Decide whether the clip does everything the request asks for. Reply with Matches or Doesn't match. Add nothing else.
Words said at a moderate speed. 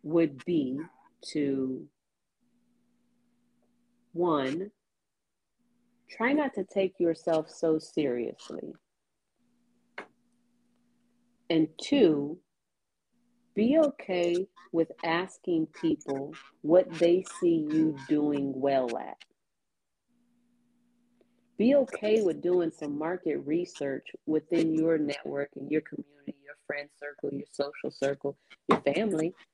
Doesn't match